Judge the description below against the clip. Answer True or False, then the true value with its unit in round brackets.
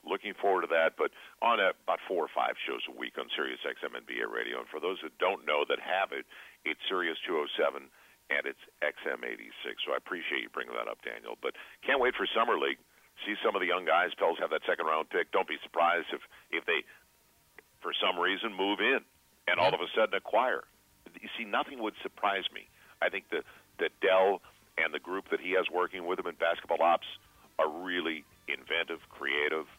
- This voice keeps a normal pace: False (210 wpm)